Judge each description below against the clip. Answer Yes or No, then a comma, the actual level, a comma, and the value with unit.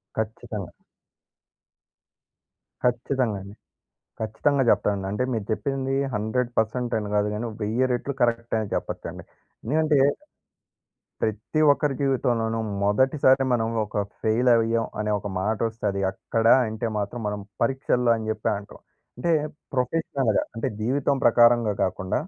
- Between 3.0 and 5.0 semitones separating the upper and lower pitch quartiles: Yes, average, 3.3 semitones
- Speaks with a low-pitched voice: Yes, low, 115 Hz